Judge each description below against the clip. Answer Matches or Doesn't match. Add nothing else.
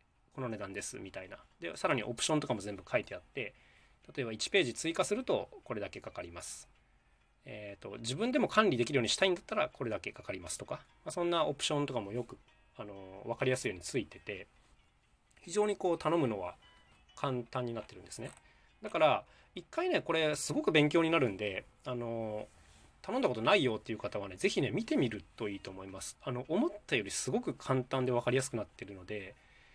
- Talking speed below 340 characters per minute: Doesn't match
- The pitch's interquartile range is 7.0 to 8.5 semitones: Matches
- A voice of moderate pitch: Doesn't match